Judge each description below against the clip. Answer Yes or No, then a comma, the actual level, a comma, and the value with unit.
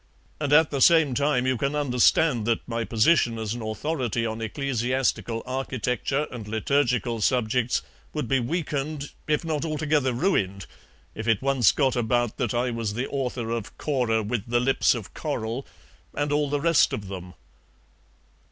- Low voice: Yes, low, 125 Hz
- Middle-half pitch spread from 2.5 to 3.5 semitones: No, average, 4.0 semitones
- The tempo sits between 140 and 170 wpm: Yes, average, 160 wpm